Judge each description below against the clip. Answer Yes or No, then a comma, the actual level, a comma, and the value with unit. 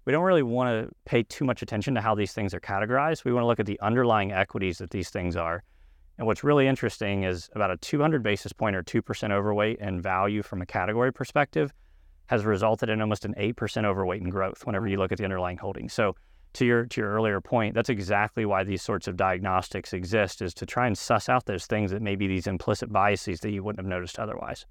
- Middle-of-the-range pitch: No, low, 105 Hz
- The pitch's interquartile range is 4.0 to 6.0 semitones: No, average, 3.3 semitones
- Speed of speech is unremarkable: No, fast, 235 wpm